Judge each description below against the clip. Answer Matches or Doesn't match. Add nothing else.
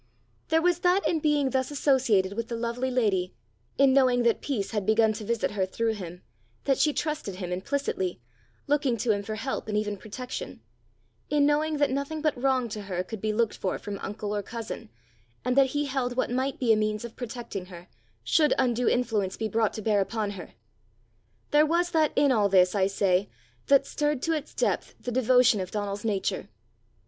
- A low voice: Doesn't match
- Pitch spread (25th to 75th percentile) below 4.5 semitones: Doesn't match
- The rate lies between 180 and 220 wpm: Matches